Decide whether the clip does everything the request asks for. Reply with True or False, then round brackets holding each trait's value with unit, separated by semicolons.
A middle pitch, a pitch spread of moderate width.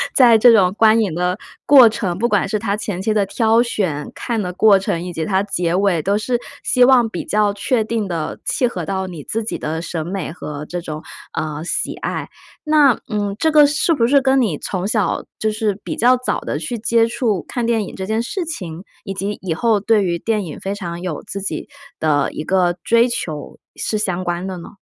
False (205 Hz; 4.5 semitones)